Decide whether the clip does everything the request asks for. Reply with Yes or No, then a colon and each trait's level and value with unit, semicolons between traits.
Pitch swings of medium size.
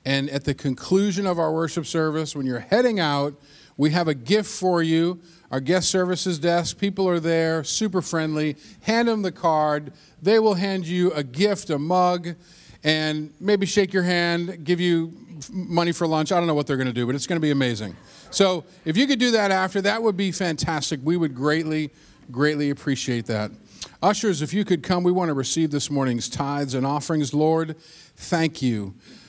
Yes: average, 3.8 semitones